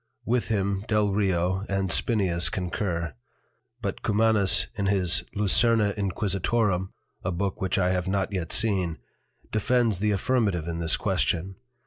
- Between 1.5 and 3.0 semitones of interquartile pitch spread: Yes, average, 2.7 semitones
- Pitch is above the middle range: No, very low, 95 Hz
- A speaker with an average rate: No, slow, 130 wpm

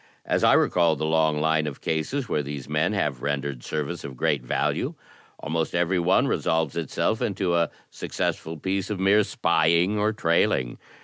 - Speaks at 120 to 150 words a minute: No, average, 170 wpm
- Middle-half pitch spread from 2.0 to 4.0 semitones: Yes, average, 3.6 semitones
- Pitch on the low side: Yes, very low, 80 Hz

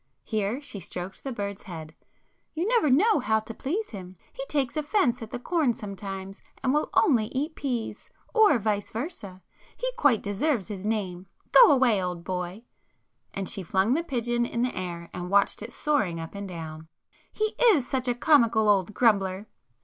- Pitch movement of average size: No, wide, 6.3 semitones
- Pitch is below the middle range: No, high, 220 Hz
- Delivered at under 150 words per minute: No, average, 165 wpm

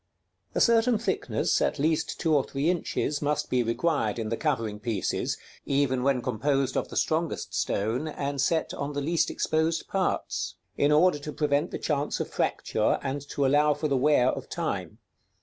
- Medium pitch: Yes, medium, 145 Hz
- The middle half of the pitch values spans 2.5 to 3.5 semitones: Yes, average, 3.1 semitones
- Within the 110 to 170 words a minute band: No, average, 185 wpm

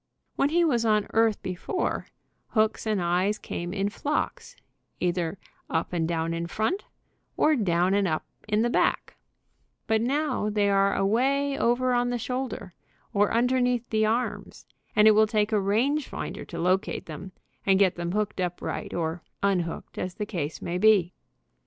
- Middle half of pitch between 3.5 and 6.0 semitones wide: Yes, average, 5.0 semitones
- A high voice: Yes, high, 210 Hz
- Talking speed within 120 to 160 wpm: No, average, 170 wpm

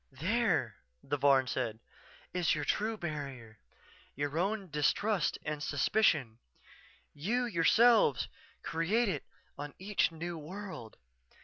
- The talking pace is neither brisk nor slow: No, slow, 110 wpm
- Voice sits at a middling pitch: Yes, medium, 160 Hz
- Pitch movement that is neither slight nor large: No, wide, 6.3 semitones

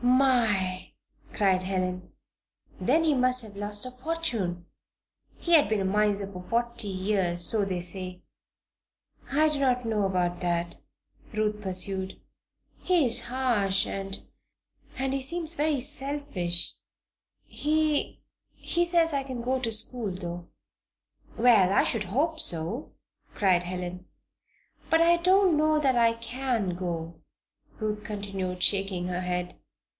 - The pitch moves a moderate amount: No, wide, 6.5 semitones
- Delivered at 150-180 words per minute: No, average, 140 wpm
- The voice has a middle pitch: No, high, 210 Hz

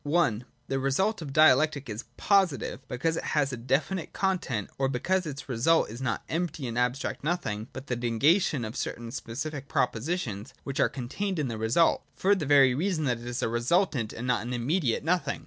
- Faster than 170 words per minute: Yes, average, 200 wpm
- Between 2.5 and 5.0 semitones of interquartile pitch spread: No, wide, 5.4 semitones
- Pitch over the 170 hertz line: No, low, 135 Hz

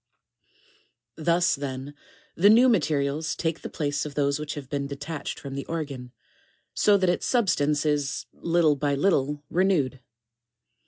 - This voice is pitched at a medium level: Yes, medium, 150 Hz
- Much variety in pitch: No, average, 3.3 semitones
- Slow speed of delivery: No, average, 150 wpm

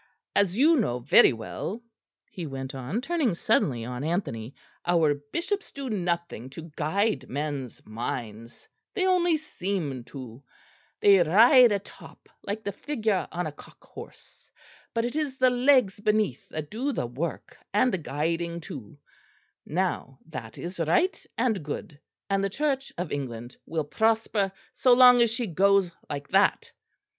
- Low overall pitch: No, medium, 180 Hz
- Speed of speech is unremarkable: Yes, average, 150 wpm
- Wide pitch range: Yes, wide, 8.1 semitones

